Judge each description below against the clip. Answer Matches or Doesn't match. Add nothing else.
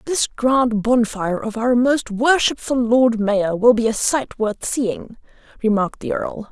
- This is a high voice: Matches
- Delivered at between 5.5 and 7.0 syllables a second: Doesn't match